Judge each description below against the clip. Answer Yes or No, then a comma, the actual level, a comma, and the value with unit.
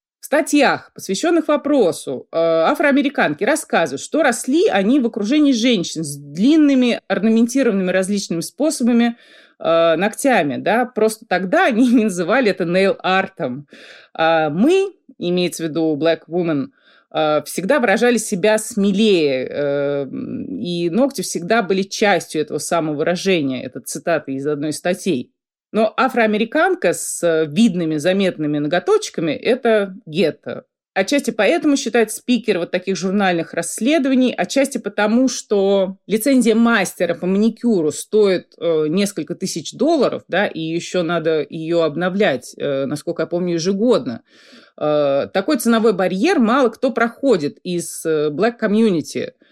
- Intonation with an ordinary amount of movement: No, wide, 6.4 semitones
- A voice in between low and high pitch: No, high, 195 Hz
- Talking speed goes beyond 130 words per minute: No, average, 120 wpm